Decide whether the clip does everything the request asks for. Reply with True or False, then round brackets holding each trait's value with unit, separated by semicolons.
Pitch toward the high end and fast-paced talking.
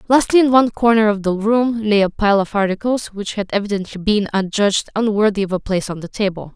True (210 Hz; 220 wpm)